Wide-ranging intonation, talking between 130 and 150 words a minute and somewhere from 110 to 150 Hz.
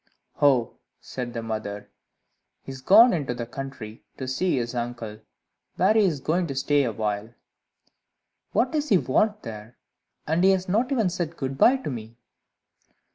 No: wide, 7.9 semitones; average, 165 wpm; low, 135 Hz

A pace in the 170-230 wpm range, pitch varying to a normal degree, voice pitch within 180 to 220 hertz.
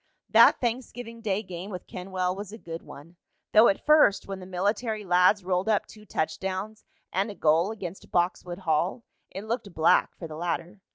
Yes: average, 180 wpm; average, 3.3 semitones; high, 190 Hz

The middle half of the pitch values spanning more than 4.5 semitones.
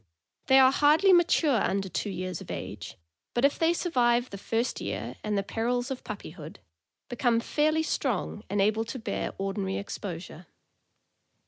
Yes: wide, 5.4 semitones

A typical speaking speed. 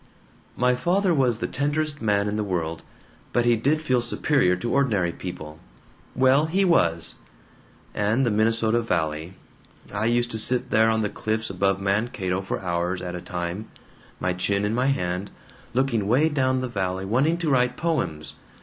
Yes: average, 170 wpm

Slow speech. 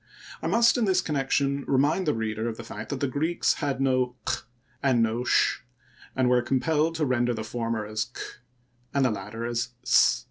No: average, 200 wpm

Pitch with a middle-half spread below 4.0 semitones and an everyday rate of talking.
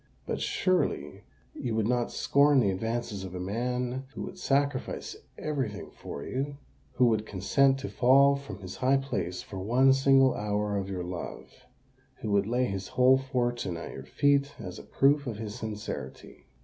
No: average, 5.0 semitones; average, 170 wpm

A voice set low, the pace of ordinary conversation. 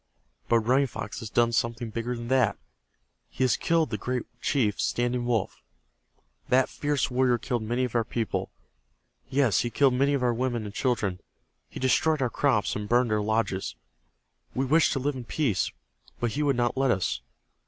Yes: low, 120 Hz; average, 185 wpm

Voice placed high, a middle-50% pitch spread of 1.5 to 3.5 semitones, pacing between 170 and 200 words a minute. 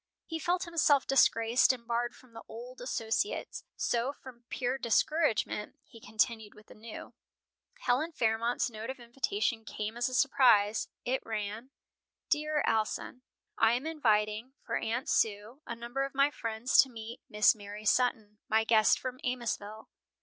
No: high, 235 Hz; average, 3.1 semitones; average, 155 wpm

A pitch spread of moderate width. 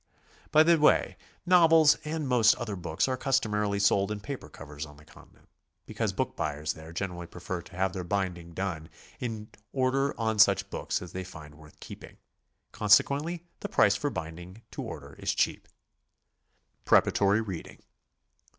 No: wide, 7.0 semitones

